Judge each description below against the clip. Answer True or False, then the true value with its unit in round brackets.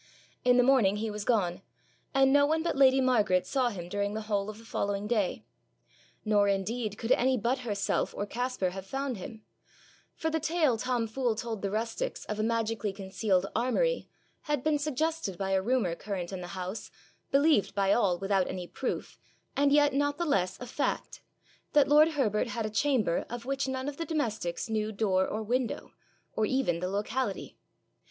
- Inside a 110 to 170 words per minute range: False (190 wpm)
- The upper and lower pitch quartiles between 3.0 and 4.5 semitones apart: False (5.0 semitones)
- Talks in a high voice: True (225 Hz)